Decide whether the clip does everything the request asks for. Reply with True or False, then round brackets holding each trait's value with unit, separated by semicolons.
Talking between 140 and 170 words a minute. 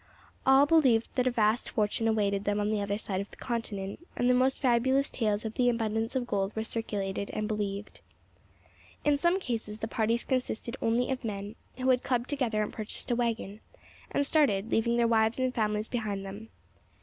False (195 wpm)